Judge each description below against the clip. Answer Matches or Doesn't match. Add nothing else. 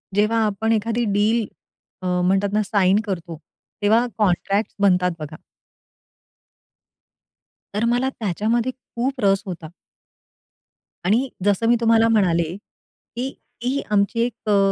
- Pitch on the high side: Matches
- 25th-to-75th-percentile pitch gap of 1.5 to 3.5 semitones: Matches